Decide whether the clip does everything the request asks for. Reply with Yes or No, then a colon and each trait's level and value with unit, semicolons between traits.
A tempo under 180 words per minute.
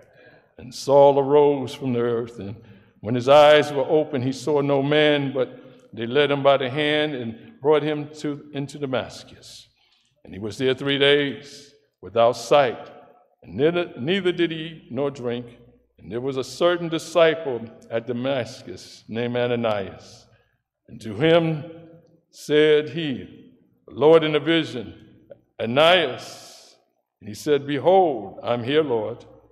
Yes: average, 150 wpm